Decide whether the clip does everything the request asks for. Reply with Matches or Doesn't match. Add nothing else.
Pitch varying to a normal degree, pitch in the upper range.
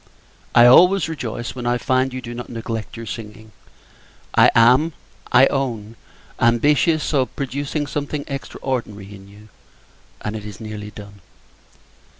Doesn't match